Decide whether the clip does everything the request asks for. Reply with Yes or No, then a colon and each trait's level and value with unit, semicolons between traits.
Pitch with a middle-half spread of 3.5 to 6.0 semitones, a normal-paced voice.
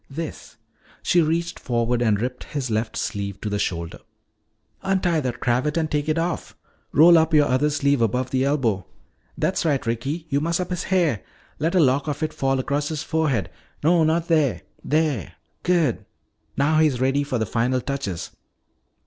Yes: average, 4.5 semitones; average, 175 wpm